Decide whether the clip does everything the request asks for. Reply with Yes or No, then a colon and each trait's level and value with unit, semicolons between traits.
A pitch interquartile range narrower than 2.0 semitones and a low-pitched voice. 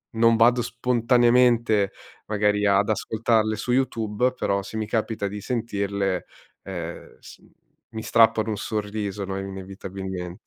No: average, 2.7 semitones; low, 105 Hz